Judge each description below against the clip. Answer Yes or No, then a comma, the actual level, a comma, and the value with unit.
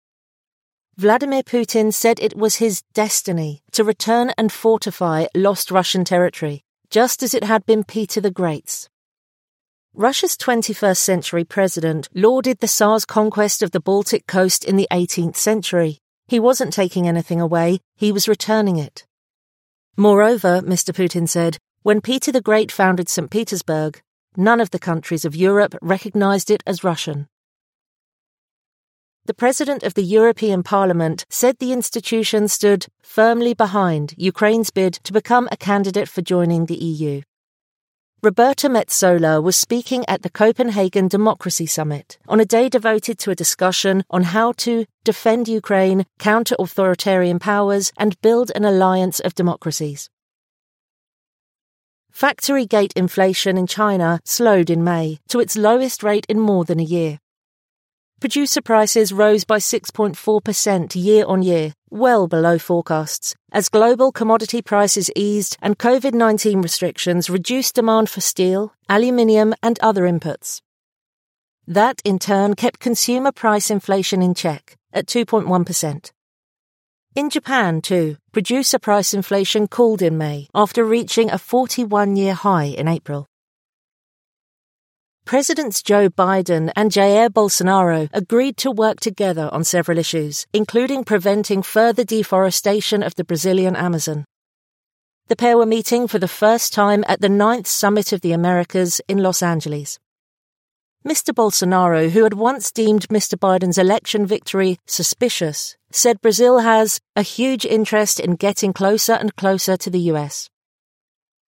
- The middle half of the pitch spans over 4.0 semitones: No, average, 3.7 semitones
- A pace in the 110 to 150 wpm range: Yes, average, 140 wpm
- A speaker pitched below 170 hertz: No, high, 205 Hz